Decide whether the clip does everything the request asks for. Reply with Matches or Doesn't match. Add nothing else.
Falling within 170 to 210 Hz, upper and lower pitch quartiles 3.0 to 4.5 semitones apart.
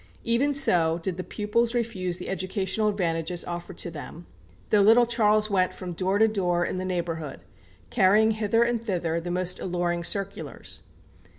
Matches